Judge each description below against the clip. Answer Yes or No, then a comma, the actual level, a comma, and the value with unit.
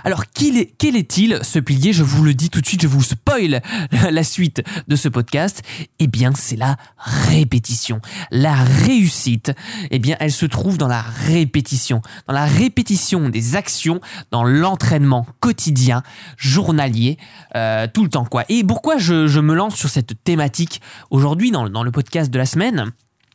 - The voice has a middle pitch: Yes, medium, 145 Hz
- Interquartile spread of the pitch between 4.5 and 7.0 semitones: Yes, average, 5.0 semitones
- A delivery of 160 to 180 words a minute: Yes, average, 175 wpm